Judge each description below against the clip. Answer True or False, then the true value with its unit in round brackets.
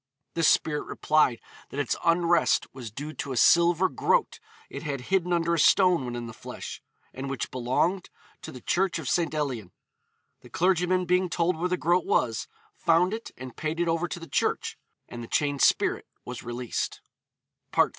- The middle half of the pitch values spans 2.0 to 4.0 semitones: False (5.2 semitones)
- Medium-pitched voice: True (160 Hz)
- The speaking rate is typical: True (190 wpm)